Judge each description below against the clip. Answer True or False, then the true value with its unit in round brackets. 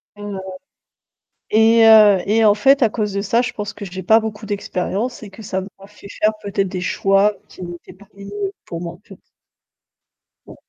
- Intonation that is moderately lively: False (1.8 semitones)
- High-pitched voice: True (205 Hz)